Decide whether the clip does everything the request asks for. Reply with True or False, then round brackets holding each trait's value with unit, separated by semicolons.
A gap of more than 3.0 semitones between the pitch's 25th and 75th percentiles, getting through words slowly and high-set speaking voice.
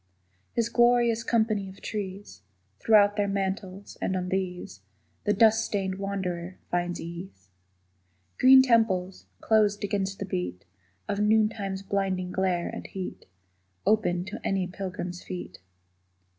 False (2.6 semitones; 130 wpm; 195 Hz)